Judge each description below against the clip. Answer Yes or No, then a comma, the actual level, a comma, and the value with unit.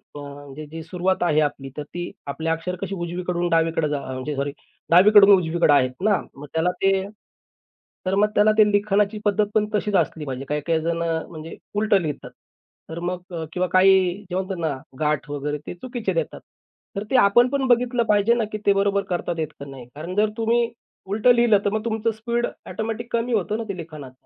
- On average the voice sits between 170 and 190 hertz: Yes, medium, 185 Hz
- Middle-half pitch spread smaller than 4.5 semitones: No, average, 5.1 semitones